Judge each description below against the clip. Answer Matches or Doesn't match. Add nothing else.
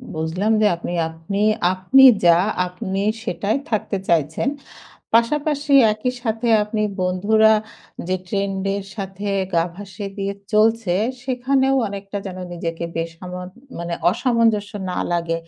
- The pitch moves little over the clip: Doesn't match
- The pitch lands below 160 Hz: Doesn't match